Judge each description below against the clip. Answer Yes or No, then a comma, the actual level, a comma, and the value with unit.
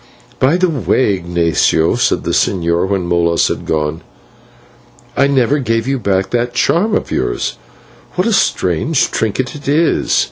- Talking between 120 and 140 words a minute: No, average, 150 wpm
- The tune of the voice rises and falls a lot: Yes, wide, 8.3 semitones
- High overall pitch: No, low, 115 Hz